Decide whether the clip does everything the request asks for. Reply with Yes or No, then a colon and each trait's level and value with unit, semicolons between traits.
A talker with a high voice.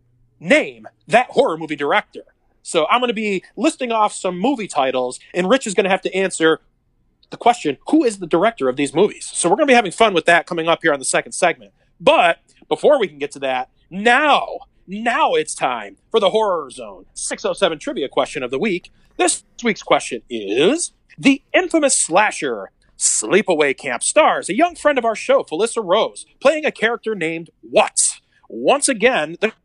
Yes: high, 210 Hz